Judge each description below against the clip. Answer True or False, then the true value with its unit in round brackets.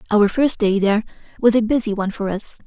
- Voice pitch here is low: False (215 Hz)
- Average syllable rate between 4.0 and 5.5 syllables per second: False (6.4 syllables/s)